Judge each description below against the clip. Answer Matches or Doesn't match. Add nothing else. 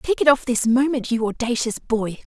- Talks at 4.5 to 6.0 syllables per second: Matches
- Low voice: Doesn't match